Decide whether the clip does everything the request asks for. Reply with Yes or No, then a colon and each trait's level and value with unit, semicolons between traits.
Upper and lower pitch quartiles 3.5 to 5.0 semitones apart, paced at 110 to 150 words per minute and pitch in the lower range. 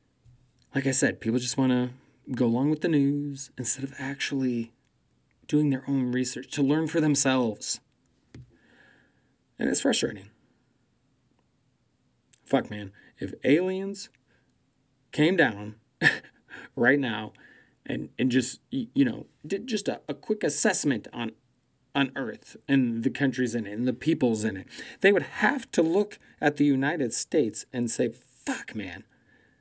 No: average, 2.7 semitones; average, 140 wpm; low, 130 Hz